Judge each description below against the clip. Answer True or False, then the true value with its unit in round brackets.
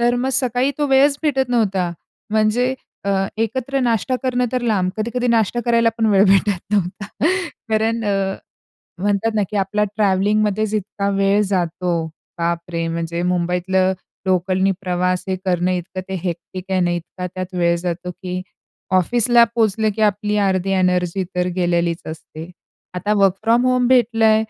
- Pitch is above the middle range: True (195 Hz)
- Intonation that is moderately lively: True (3.8 semitones)